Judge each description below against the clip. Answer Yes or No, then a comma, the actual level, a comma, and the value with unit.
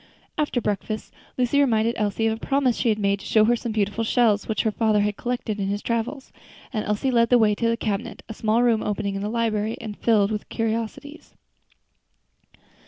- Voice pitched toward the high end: Yes, high, 220 Hz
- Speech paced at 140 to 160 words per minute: No, fast, 205 wpm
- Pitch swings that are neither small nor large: No, narrow, 2.0 semitones